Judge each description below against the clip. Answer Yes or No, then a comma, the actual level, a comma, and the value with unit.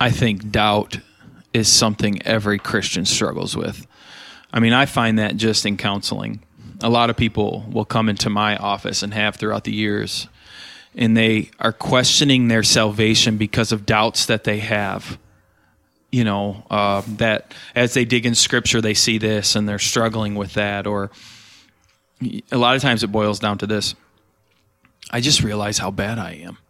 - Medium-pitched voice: No, low, 110 Hz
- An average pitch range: No, narrow, 1.9 semitones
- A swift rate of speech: No, average, 175 wpm